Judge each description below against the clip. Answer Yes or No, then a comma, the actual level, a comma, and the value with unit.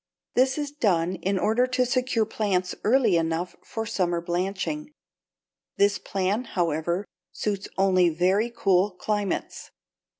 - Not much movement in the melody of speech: No, average, 4.3 semitones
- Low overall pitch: No, high, 200 Hz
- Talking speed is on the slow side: Yes, slow, 125 wpm